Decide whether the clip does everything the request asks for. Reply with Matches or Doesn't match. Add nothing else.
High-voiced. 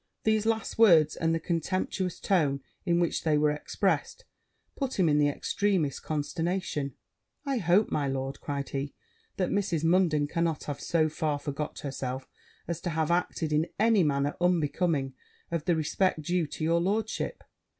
Doesn't match